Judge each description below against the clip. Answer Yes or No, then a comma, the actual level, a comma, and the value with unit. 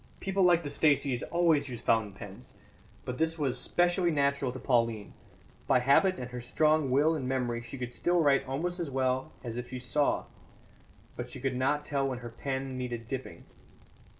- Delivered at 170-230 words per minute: Yes, average, 185 wpm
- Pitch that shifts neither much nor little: Yes, average, 3.6 semitones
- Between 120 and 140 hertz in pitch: Yes, low, 135 Hz